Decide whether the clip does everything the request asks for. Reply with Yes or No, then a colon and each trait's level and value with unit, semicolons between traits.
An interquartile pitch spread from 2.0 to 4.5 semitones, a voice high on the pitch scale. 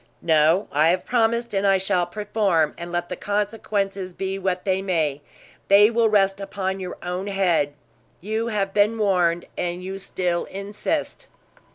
Yes: narrow, 2.6 semitones; high, 195 Hz